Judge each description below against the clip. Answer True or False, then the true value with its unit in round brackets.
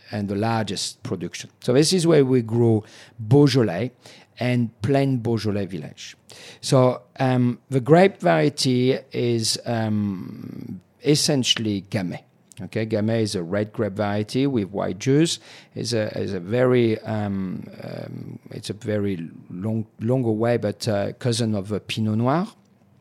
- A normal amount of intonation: True (3.7 semitones)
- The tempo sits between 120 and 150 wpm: True (140 wpm)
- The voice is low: True (115 Hz)